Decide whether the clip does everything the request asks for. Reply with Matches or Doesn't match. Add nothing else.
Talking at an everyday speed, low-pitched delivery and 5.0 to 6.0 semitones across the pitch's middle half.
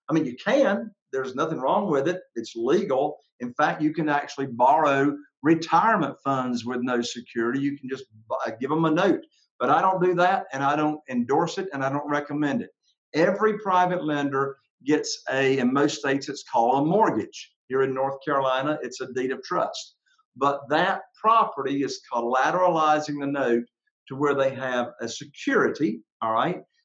Doesn't match